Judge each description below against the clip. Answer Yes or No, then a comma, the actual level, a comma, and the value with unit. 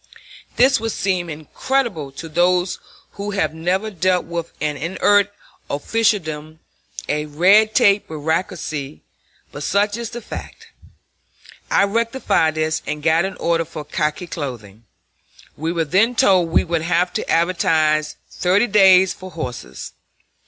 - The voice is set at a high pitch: No, medium, 175 Hz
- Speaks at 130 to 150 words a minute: Yes, slow, 135 wpm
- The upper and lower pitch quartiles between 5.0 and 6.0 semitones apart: No, average, 4.3 semitones